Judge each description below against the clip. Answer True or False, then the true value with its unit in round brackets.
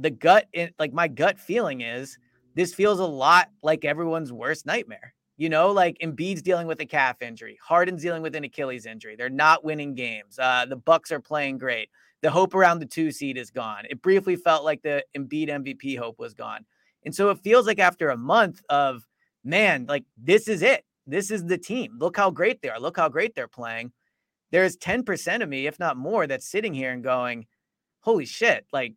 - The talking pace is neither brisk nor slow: False (210 wpm)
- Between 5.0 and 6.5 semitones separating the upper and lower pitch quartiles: True (5.3 semitones)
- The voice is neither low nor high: True (155 Hz)